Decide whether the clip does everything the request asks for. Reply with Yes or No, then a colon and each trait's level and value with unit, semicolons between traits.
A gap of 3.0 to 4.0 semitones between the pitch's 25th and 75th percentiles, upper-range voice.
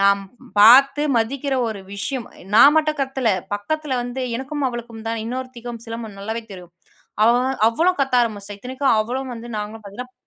Yes: average, 3.3 semitones; high, 240 Hz